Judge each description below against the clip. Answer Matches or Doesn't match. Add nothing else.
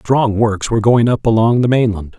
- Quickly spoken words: Matches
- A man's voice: Matches